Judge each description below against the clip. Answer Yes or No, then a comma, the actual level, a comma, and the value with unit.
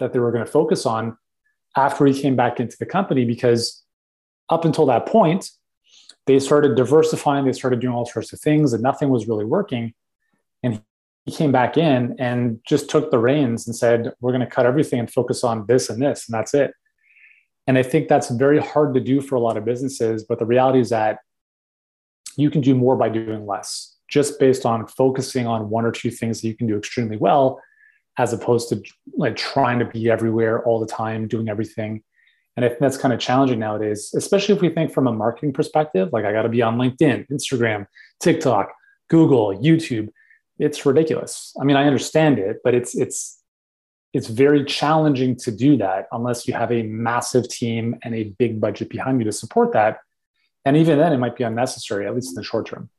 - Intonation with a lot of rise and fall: No, average, 3.9 semitones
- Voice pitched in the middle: No, low, 125 Hz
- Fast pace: Yes, fast, 210 wpm